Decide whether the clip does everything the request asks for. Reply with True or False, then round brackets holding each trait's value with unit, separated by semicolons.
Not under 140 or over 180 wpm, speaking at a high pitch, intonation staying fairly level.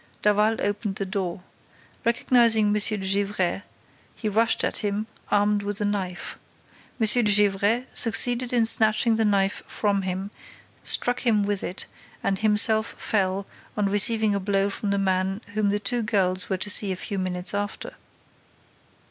True (160 wpm; 205 Hz; 1.9 semitones)